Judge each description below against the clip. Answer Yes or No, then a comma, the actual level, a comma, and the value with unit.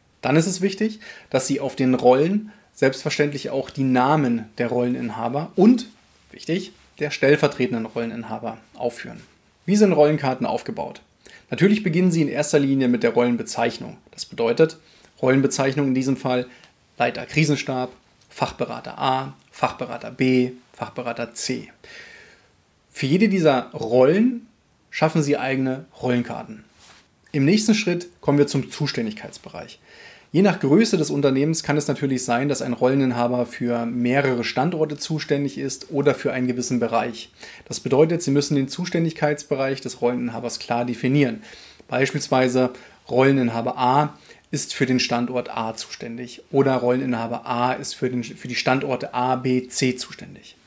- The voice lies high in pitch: No, low, 135 Hz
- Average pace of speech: Yes, average, 140 wpm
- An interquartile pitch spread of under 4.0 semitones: Yes, average, 3.2 semitones